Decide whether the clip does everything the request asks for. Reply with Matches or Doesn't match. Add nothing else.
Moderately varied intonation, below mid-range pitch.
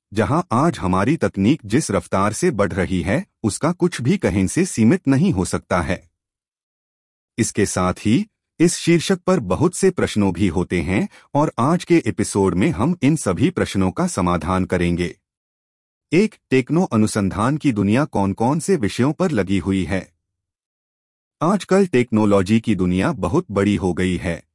Doesn't match